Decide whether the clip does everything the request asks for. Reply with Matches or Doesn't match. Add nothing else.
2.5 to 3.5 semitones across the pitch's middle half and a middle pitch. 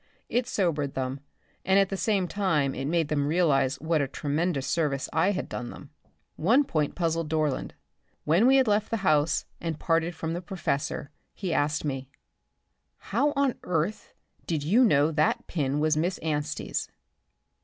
Doesn't match